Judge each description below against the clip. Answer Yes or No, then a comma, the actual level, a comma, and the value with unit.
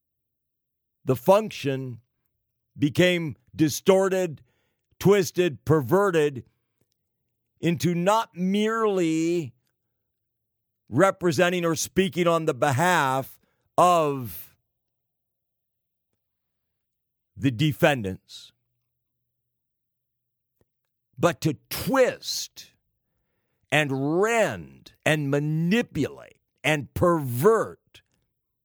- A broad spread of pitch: Yes, wide, 6.1 semitones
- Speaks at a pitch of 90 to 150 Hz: Yes, low, 135 Hz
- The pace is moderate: No, slow, 55 wpm